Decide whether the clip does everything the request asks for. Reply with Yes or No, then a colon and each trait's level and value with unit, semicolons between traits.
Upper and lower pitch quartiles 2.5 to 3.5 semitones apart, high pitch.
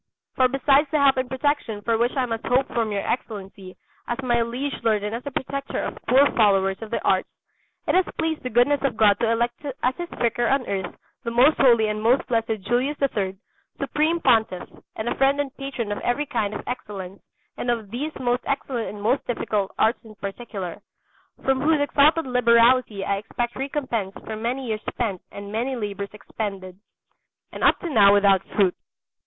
No: average, 4.2 semitones; high, 235 Hz